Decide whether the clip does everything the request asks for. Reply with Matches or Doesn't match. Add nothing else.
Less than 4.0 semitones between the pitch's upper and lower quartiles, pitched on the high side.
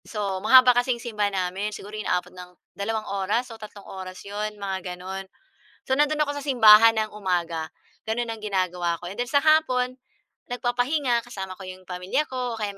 Doesn't match